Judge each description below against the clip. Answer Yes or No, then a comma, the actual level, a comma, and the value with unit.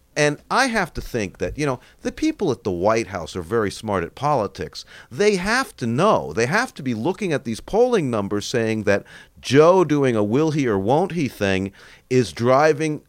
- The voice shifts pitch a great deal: Yes, wide, 8.9 semitones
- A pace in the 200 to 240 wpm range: Yes, fast, 205 wpm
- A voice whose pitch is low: Yes, low, 130 Hz